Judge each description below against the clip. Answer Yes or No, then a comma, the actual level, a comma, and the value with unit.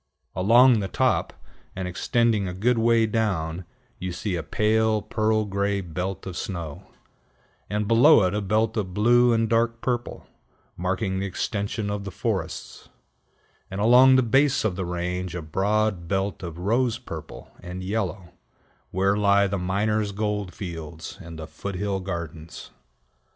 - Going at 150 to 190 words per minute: Yes, average, 155 wpm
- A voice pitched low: Yes, low, 100 Hz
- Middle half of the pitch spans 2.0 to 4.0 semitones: Yes, average, 3.4 semitones